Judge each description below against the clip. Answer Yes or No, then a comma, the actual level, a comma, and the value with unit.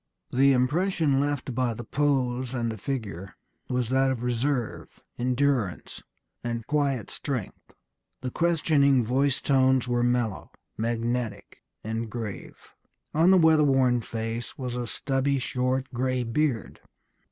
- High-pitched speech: No, low, 125 Hz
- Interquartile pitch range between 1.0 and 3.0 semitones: Yes, average, 2.7 semitones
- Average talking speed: No, slow, 125 wpm